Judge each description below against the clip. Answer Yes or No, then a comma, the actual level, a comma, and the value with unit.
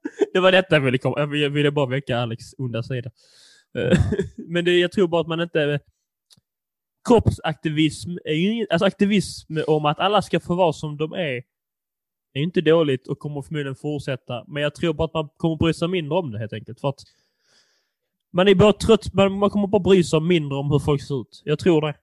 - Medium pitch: Yes, medium, 155 Hz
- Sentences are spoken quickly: Yes, fast, 205 wpm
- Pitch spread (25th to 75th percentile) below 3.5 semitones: No, average, 4.2 semitones